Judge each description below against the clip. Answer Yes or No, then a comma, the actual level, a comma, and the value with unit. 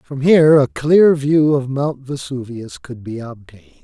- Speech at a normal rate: Yes, average, 170 wpm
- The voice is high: No, low, 135 Hz